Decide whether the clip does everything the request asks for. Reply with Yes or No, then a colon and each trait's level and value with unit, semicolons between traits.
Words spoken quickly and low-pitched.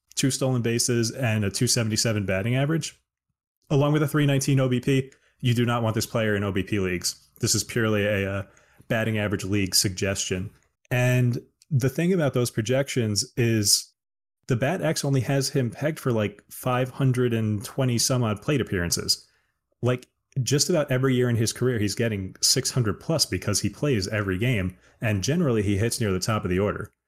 No: average, 175 wpm; low, 120 Hz